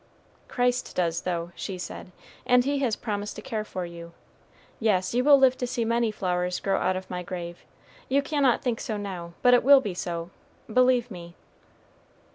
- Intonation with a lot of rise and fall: Yes, wide, 5.7 semitones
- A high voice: Yes, high, 210 Hz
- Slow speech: No, average, 185 wpm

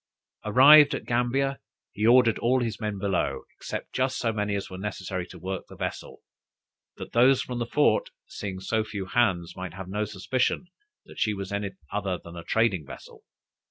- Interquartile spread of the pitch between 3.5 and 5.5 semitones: Yes, average, 4.2 semitones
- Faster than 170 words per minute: Yes, average, 185 wpm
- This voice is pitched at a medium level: No, low, 105 Hz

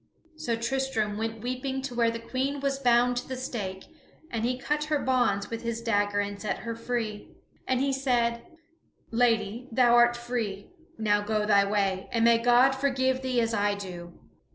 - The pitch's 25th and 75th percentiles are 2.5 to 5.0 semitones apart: Yes, average, 3.4 semitones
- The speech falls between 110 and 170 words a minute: No, average, 180 wpm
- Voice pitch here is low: No, high, 235 Hz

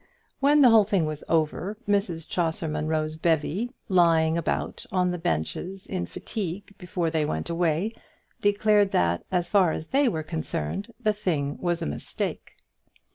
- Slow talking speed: No, average, 155 wpm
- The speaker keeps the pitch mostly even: No, average, 4.3 semitones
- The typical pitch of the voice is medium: Yes, medium, 175 Hz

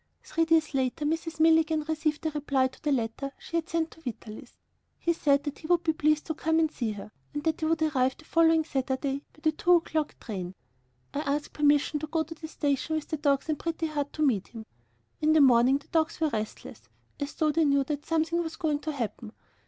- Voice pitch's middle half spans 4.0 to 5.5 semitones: No, narrow, 2.5 semitones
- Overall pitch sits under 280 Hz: No, very high, 300 Hz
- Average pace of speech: No, fast, 225 wpm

